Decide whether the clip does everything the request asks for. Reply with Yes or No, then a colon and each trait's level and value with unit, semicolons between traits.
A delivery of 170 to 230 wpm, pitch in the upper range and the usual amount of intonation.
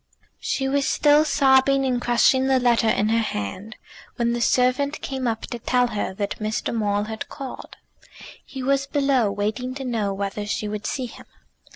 Yes: average, 180 wpm; high, 245 Hz; average, 3.9 semitones